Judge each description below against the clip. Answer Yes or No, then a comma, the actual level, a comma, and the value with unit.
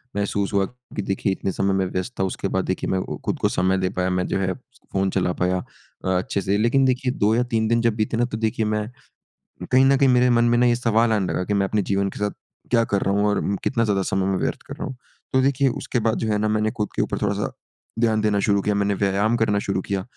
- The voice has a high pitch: No, low, 105 Hz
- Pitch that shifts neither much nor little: Yes, average, 3.3 semitones